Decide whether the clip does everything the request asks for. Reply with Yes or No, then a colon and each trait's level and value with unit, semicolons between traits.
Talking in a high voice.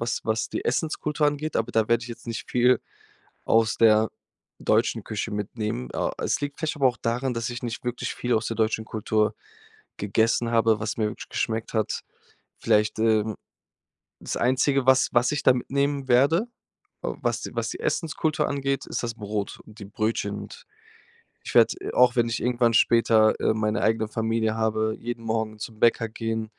No: low, 115 Hz